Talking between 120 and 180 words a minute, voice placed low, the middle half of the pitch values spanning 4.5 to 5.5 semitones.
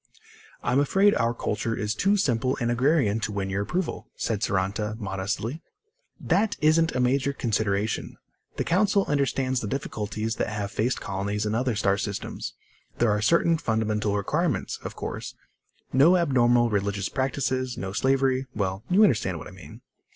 Yes: average, 160 wpm; low, 115 Hz; average, 4.9 semitones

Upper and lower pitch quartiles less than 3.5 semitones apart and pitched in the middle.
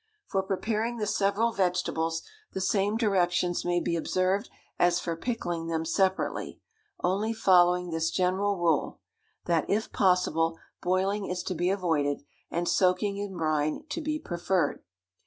Yes: average, 2.8 semitones; medium, 180 Hz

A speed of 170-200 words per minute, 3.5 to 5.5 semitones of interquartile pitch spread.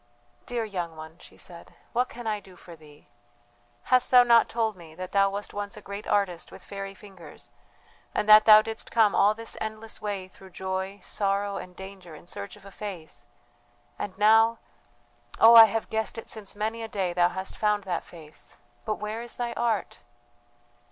No: average, 190 wpm; average, 2.9 semitones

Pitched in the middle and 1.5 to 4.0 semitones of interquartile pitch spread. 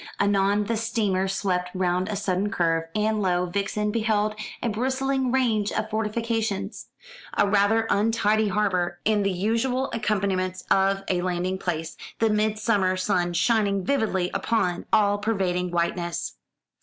No: high, 205 Hz; average, 2.9 semitones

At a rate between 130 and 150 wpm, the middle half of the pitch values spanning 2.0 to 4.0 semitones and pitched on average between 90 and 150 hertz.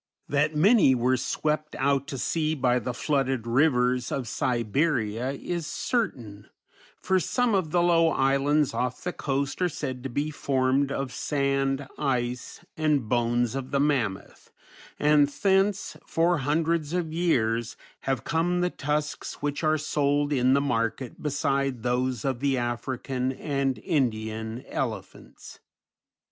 Yes: average, 140 wpm; average, 3.4 semitones; medium, 140 Hz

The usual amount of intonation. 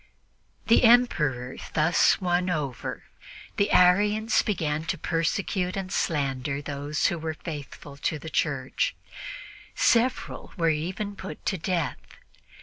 Yes: average, 4.5 semitones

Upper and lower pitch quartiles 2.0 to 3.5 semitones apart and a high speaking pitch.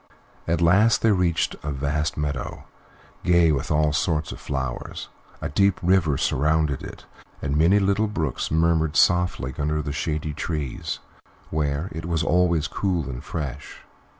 No: average, 3.1 semitones; very low, 80 Hz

